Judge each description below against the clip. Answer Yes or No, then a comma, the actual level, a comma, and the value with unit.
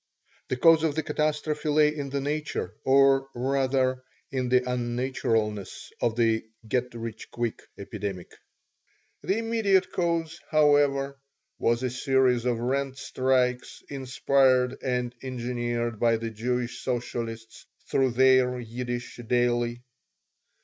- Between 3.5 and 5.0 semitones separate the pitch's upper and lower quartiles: No, narrow, 2.5 semitones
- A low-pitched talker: Yes, low, 125 Hz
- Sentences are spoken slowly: Yes, slow, 120 wpm